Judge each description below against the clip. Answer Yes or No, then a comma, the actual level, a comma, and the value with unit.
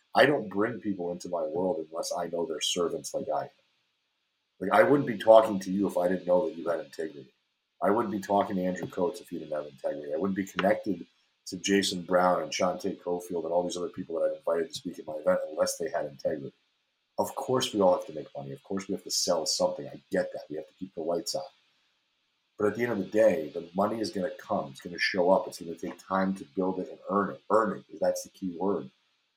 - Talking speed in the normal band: No, fast, 265 wpm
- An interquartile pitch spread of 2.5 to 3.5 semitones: Yes, average, 3.0 semitones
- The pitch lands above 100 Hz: No, very low, 95 Hz